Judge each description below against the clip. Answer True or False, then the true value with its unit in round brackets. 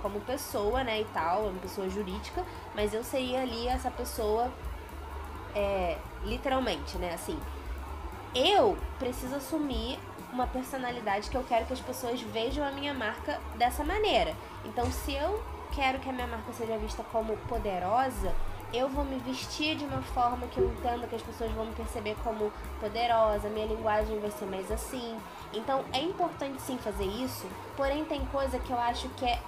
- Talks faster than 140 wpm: True (175 wpm)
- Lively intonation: False (3.7 semitones)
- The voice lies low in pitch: False (240 Hz)